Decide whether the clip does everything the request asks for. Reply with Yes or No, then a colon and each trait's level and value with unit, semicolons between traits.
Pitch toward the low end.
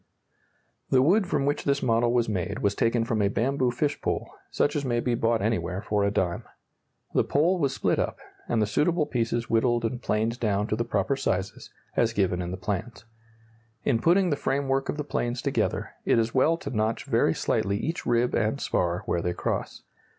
Yes: low, 115 Hz